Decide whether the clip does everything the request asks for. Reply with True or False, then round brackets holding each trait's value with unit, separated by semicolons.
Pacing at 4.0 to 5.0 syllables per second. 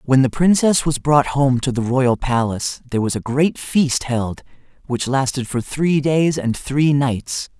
True (4.2 syllables/s)